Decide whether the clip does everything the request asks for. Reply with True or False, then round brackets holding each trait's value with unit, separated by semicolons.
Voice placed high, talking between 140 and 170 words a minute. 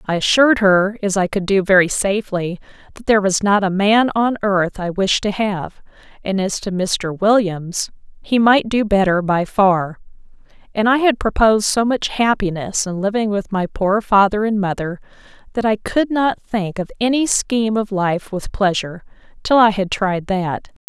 False (205 Hz; 185 wpm)